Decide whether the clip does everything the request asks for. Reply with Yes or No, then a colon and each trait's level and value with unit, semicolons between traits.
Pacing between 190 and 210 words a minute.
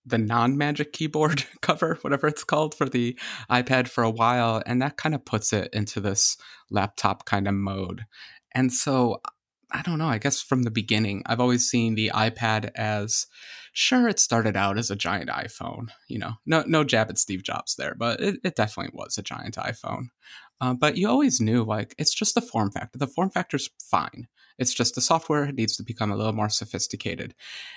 Yes: average, 200 wpm